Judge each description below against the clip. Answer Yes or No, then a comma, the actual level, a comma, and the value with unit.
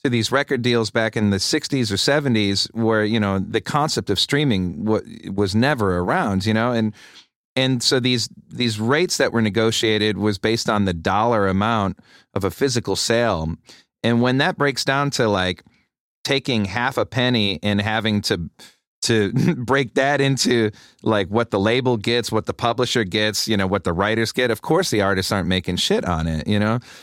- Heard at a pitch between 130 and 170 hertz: No, low, 110 Hz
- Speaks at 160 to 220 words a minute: Yes, average, 190 wpm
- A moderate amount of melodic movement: Yes, average, 3.6 semitones